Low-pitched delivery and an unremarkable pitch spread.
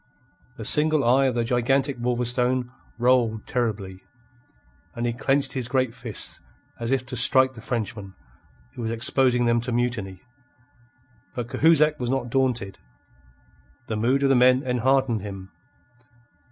No: low, 125 Hz; narrow, 2.2 semitones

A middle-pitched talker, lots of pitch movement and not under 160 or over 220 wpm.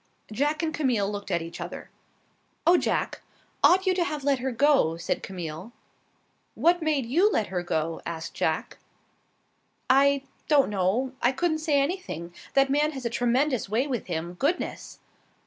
No: very high, 265 Hz; wide, 7.6 semitones; average, 165 wpm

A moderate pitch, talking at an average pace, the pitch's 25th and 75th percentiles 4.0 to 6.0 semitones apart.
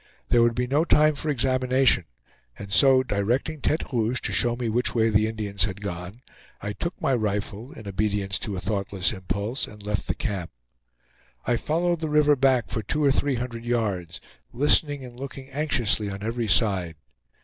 No: low, 115 Hz; average, 180 wpm; average, 4.8 semitones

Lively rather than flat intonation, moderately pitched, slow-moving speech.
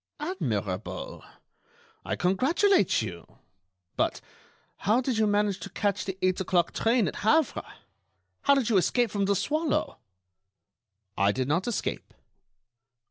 No: wide, 5.9 semitones; high, 205 Hz; slow, 130 wpm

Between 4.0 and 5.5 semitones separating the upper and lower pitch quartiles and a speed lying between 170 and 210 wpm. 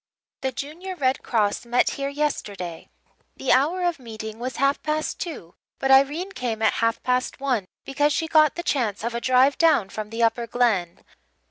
Yes: average, 4.6 semitones; average, 180 wpm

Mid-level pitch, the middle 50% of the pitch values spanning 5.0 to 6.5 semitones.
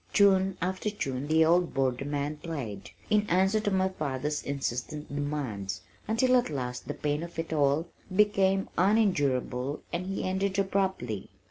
Yes: medium, 160 Hz; wide, 5.5 semitones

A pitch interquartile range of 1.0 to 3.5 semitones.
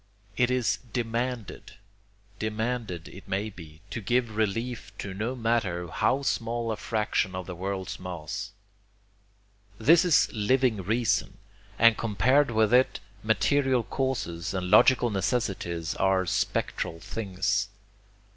No: average, 4.5 semitones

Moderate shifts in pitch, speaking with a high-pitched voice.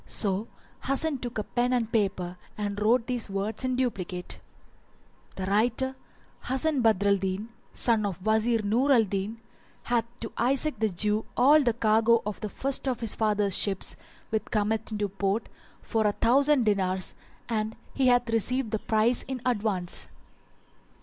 Yes: average, 3.2 semitones; high, 220 Hz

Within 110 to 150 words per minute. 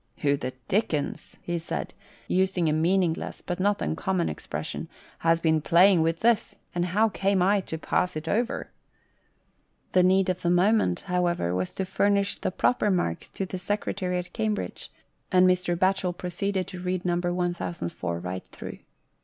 No: average, 165 wpm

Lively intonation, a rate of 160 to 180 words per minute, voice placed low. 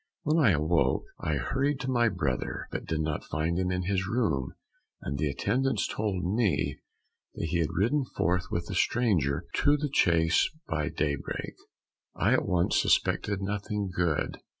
Yes: wide, 5.7 semitones; average, 165 wpm; very low, 90 Hz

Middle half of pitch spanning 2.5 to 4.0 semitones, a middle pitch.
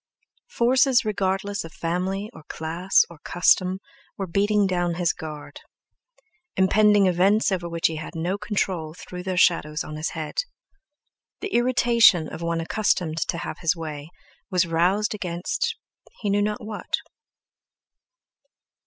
Yes: average, 3.7 semitones; medium, 180 Hz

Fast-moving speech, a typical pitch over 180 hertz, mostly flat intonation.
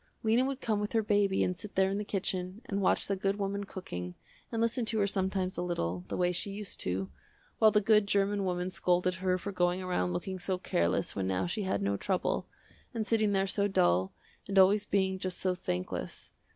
Yes: fast, 215 wpm; high, 190 Hz; narrow, 2.3 semitones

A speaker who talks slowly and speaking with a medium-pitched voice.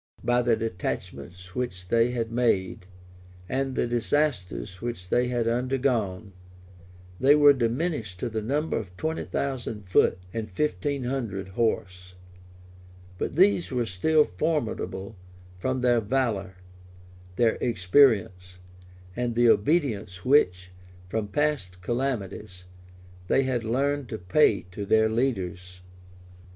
No: slow, 120 wpm; low, 115 Hz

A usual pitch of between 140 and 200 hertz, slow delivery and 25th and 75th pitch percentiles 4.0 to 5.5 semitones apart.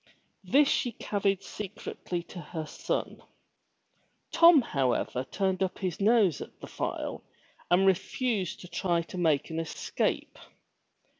No: medium, 185 Hz; slow, 130 wpm; average, 3.6 semitones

